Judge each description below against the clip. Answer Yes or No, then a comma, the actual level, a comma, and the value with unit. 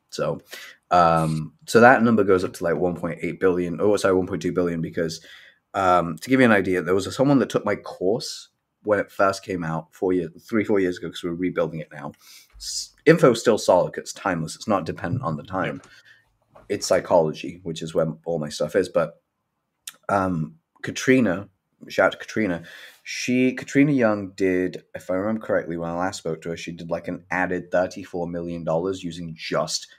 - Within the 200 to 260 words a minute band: Yes, fast, 205 wpm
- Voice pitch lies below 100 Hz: Yes, very low, 90 Hz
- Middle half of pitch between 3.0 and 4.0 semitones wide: No, narrow, 2.5 semitones